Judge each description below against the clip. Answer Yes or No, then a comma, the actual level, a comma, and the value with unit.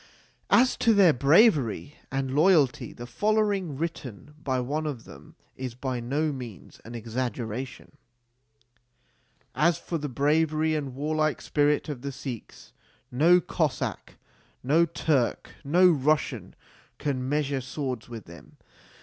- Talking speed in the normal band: No, slow, 125 wpm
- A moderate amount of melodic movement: Yes, average, 3.7 semitones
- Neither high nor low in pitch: Yes, medium, 145 Hz